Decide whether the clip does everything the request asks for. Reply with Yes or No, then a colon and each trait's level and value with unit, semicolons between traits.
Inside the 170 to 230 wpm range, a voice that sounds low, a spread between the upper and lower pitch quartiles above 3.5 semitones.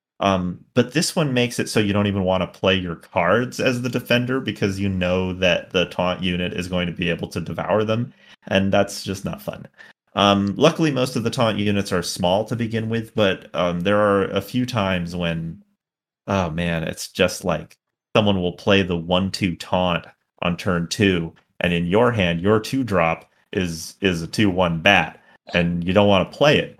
Yes: fast, 205 wpm; low, 100 Hz; average, 4.0 semitones